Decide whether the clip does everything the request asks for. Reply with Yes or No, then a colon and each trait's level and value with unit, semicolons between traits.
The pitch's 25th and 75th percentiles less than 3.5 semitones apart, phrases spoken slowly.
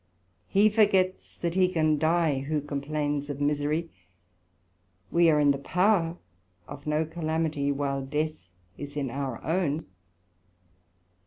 Yes: average, 2.8 semitones; slow, 130 wpm